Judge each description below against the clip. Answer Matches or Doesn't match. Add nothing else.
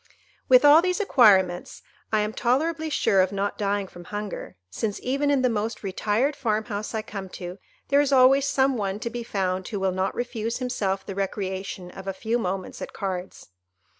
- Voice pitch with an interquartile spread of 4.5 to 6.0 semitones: Matches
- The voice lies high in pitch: Matches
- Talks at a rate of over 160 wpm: Matches